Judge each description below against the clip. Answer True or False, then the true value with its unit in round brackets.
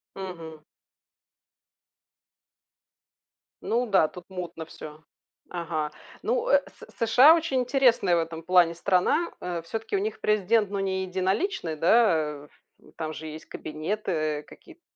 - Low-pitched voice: False (185 Hz)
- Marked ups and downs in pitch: True (6.1 semitones)